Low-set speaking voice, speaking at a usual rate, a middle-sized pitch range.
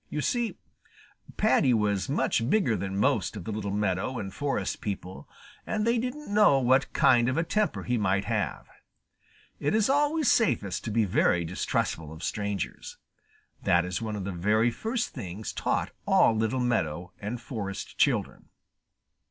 No: low, 110 Hz; average, 160 wpm; wide, 6.7 semitones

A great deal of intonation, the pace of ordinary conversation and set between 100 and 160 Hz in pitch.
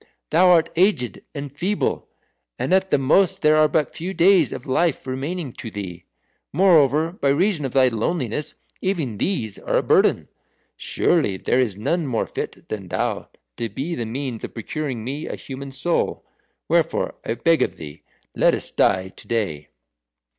Yes: wide, 6.3 semitones; average, 170 wpm; medium, 140 Hz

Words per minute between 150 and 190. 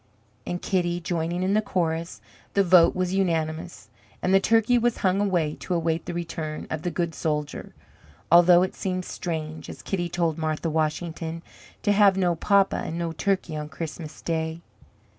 Yes: average, 170 wpm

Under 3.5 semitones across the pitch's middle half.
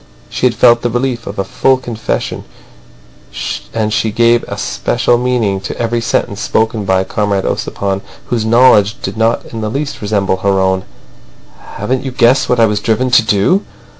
Yes: average, 3.1 semitones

